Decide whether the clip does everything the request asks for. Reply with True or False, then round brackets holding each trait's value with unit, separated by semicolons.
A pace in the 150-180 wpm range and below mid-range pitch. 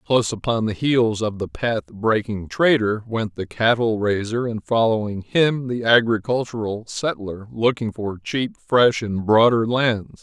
True (155 wpm; 115 Hz)